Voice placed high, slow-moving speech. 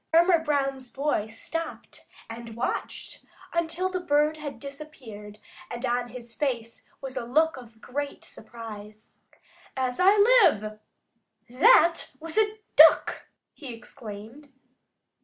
Yes: very high, 270 Hz; slow, 120 wpm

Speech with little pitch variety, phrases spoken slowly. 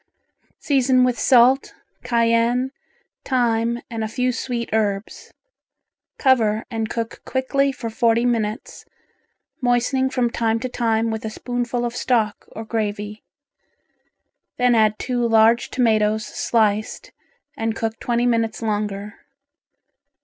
Yes: narrow, 2.0 semitones; slow, 120 wpm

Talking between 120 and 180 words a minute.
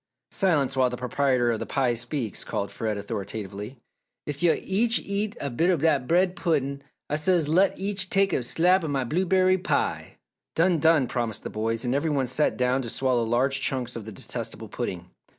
No: average, 195 wpm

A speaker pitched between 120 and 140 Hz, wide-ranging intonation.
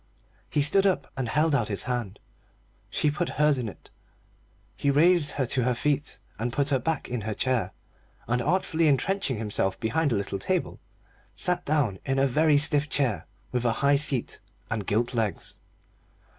No: low, 135 Hz; average, 4.5 semitones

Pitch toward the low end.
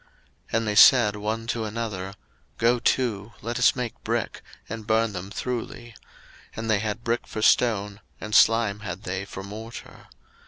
Yes: low, 110 Hz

